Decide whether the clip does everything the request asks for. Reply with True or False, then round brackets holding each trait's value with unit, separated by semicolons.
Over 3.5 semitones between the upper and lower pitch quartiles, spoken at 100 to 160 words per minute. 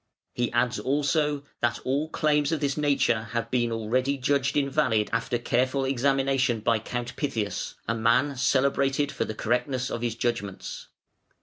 False (3.0 semitones; 150 wpm)